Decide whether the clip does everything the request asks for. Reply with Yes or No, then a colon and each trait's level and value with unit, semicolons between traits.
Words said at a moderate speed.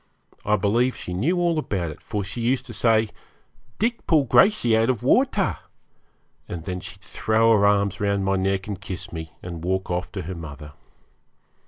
Yes: average, 185 wpm